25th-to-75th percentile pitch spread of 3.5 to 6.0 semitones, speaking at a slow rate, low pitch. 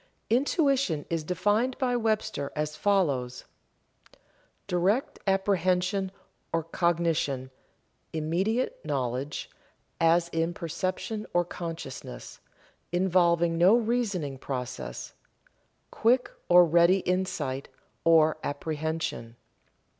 No: average, 4.1 semitones; slow, 85 wpm; medium, 170 Hz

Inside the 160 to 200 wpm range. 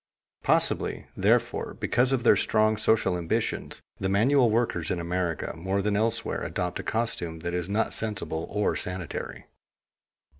No: average, 145 wpm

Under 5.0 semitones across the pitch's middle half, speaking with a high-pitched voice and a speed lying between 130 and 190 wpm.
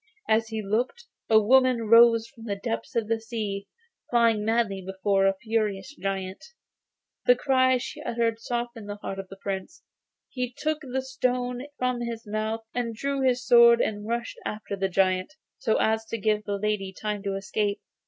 Yes: average, 3.1 semitones; high, 225 Hz; average, 175 wpm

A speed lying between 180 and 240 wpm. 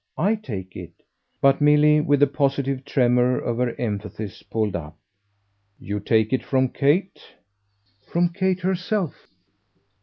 No: average, 140 wpm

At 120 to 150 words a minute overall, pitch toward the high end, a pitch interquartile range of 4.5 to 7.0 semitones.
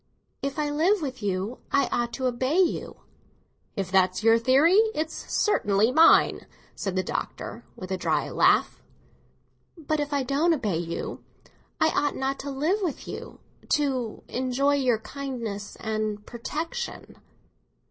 Yes: average, 140 wpm; very high, 260 Hz; wide, 5.5 semitones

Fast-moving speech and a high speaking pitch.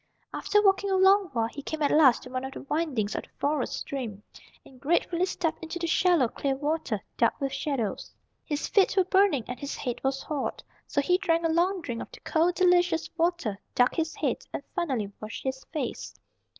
Yes: fast, 210 wpm; very high, 305 Hz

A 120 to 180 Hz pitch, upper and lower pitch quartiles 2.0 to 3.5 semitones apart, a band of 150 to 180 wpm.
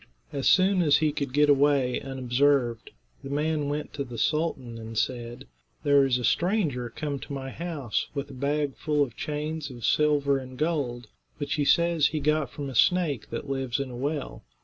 No: medium, 140 Hz; average, 2.8 semitones; average, 195 wpm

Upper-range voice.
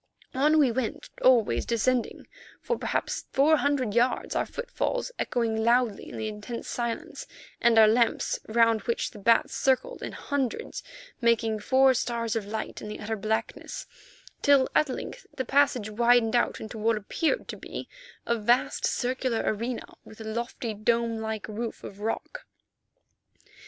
Yes: high, 235 Hz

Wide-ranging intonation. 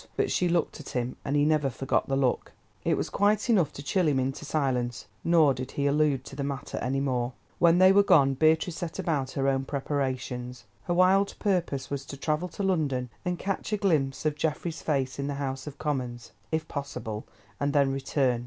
No: average, 3.5 semitones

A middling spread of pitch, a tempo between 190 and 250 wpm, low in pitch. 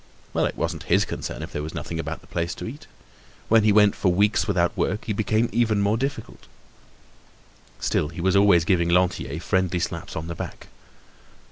Yes: average, 4.0 semitones; average, 195 wpm; very low, 95 Hz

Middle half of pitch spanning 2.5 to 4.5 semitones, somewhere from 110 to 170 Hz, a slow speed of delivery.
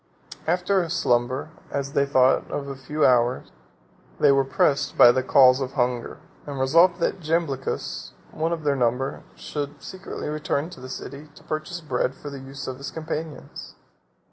No: average, 3.1 semitones; medium, 140 Hz; average, 170 wpm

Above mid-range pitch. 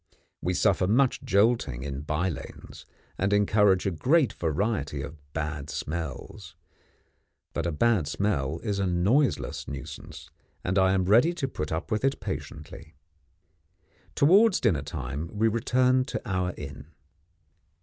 No: very low, 95 Hz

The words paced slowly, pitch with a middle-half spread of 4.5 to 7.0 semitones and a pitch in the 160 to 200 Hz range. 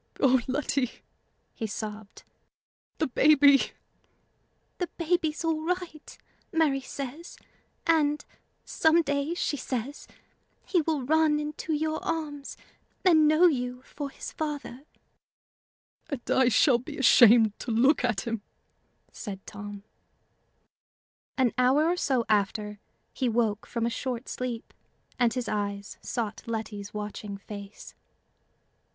No: slow, 120 wpm; wide, 5.4 semitones; very high, 260 Hz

